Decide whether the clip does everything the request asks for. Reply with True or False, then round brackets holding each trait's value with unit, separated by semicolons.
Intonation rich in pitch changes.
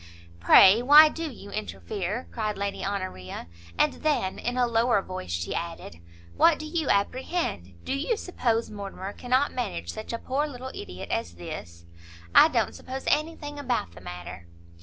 True (8.4 semitones)